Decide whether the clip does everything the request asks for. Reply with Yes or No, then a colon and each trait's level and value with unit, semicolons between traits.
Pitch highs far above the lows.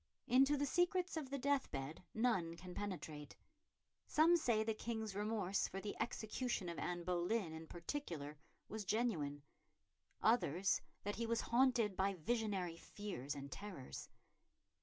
Yes: wide, 5.8 semitones